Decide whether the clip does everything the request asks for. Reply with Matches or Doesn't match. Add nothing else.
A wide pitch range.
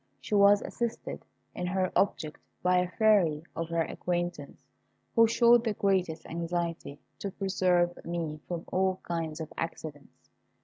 Doesn't match